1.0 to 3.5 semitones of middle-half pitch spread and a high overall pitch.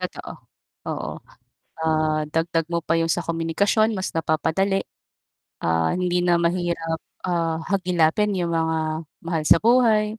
No: narrow, 2.5 semitones; medium, 170 Hz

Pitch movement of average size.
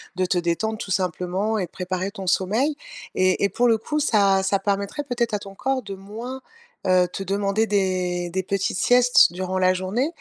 Yes: average, 3.1 semitones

